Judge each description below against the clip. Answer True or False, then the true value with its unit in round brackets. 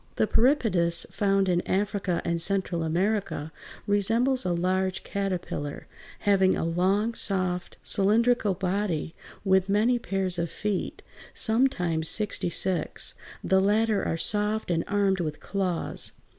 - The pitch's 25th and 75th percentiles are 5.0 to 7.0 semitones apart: False (2.8 semitones)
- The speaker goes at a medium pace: False (125 wpm)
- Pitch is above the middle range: True (195 Hz)